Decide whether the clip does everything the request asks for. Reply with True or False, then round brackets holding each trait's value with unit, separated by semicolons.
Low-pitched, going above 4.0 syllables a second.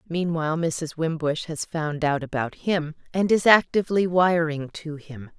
False (160 Hz; 4.5 syllables/s)